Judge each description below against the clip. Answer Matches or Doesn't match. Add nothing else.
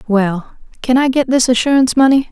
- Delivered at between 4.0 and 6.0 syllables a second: Matches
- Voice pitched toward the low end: Doesn't match